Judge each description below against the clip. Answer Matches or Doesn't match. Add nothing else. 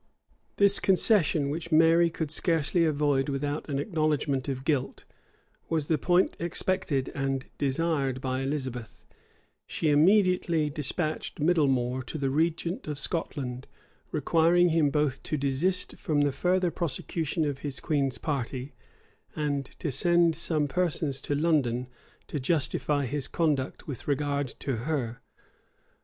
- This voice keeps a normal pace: Doesn't match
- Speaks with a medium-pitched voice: Matches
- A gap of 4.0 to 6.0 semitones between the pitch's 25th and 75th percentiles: Doesn't match